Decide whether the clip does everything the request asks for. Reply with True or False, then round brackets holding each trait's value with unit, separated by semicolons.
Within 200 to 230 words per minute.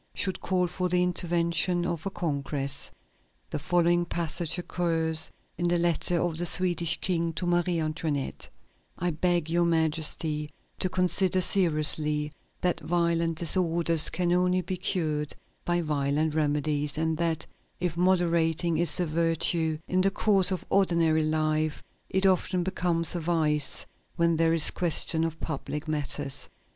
False (145 wpm)